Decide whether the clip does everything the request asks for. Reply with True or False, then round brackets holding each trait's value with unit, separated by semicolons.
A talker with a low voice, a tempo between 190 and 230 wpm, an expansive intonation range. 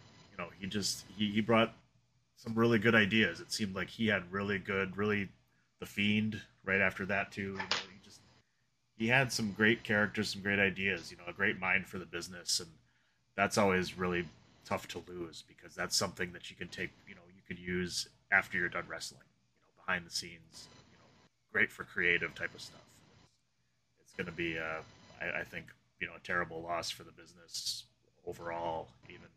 False (100 Hz; 205 wpm; 3.7 semitones)